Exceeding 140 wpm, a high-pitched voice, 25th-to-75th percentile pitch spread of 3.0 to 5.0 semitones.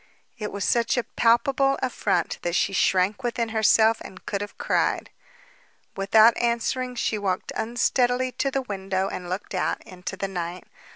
Yes: average, 160 wpm; high, 220 Hz; average, 4.0 semitones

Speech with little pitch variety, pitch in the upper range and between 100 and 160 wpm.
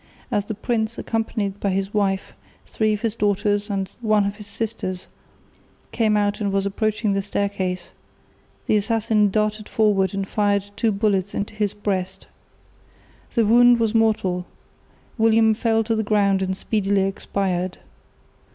Yes: narrow, 1.9 semitones; high, 205 Hz; average, 150 wpm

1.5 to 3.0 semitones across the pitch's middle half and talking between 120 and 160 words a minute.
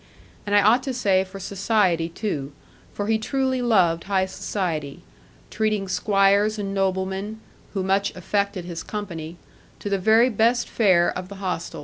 Yes: narrow, 2.6 semitones; average, 155 wpm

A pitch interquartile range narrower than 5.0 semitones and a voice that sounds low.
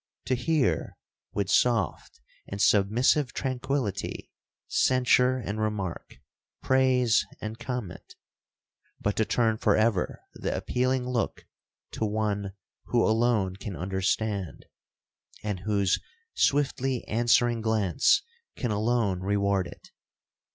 Yes: average, 3.8 semitones; low, 110 Hz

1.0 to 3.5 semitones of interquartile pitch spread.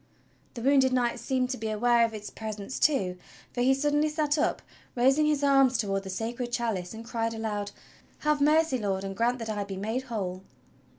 No: average, 4.2 semitones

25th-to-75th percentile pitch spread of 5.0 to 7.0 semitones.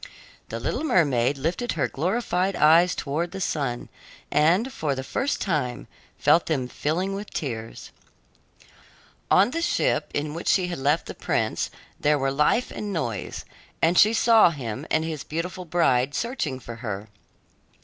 Yes: wide, 5.5 semitones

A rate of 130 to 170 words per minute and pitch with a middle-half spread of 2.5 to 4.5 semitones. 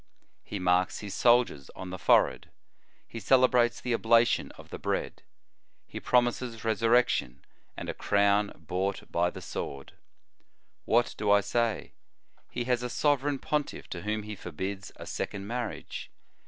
Yes: average, 145 wpm; average, 3.9 semitones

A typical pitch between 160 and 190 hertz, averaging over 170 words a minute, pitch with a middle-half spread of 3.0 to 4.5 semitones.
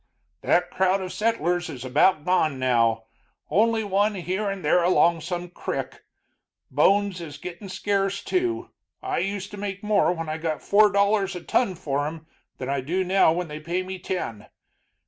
Yes: medium, 185 Hz; average, 180 wpm; average, 3.9 semitones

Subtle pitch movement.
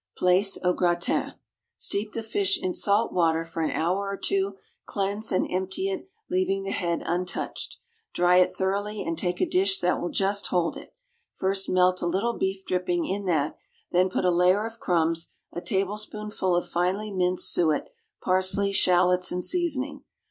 Yes: narrow, 2.0 semitones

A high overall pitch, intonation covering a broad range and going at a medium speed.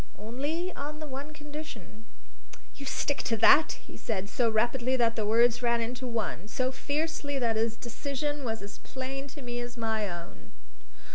No: high, 245 Hz; average, 4.1 semitones; average, 170 wpm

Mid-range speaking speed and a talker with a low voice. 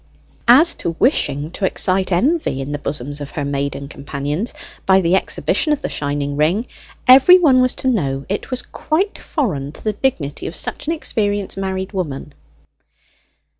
No: average, 170 wpm; high, 190 Hz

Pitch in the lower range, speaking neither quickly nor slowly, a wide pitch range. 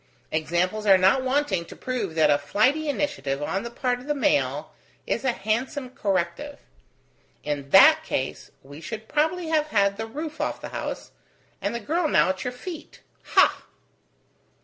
No: high, 220 Hz; average, 170 wpm; wide, 8.7 semitones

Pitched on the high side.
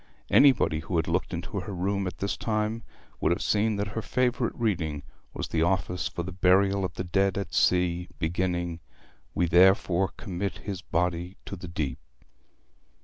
No: very low, 90 Hz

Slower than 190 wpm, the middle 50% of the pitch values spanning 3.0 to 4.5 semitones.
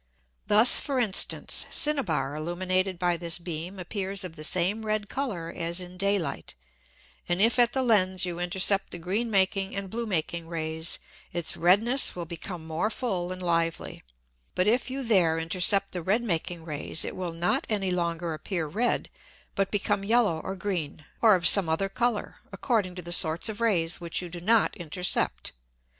Yes: average, 180 wpm; average, 3.5 semitones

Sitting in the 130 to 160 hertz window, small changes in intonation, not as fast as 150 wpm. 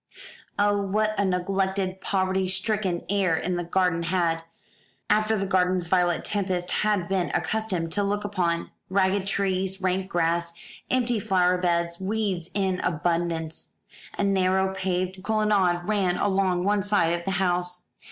No: medium, 185 Hz; narrow, 2.1 semitones; average, 140 wpm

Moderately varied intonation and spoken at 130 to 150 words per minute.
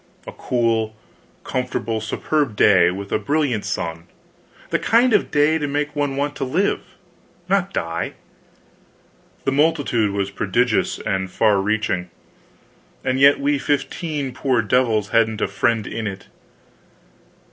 No: wide, 5.8 semitones; slow, 135 wpm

